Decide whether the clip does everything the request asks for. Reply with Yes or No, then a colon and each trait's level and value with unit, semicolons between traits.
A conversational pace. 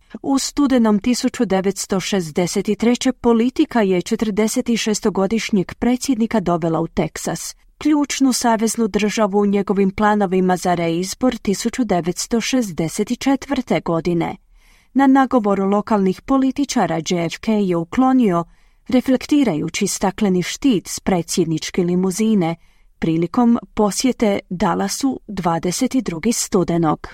No: slow, 85 wpm